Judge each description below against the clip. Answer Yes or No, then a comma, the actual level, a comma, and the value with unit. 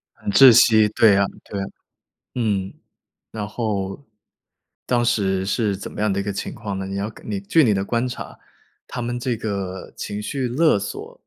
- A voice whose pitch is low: Yes, low, 105 Hz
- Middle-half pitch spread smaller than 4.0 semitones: Yes, average, 3.3 semitones